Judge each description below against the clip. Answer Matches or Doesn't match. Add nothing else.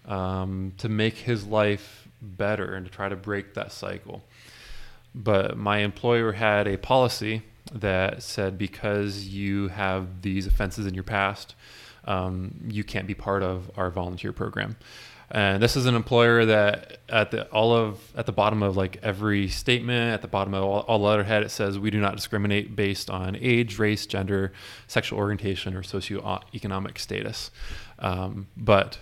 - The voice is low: Matches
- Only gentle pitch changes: Matches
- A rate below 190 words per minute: Matches